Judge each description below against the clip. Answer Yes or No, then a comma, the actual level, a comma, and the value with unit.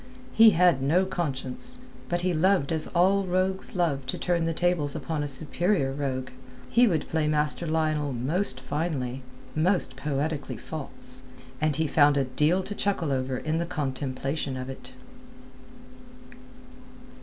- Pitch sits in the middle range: Yes, medium, 155 Hz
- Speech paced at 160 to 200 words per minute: No, average, 145 wpm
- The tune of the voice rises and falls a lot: No, average, 4.5 semitones